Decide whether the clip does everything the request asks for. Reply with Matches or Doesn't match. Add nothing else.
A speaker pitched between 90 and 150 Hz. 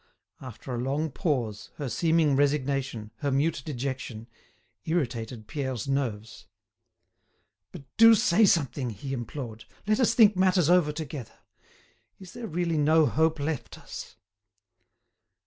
Matches